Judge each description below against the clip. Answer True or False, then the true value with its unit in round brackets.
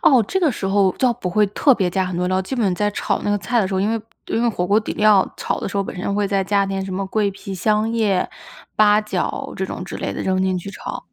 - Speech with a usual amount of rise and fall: False (2.2 semitones)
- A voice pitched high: True (200 Hz)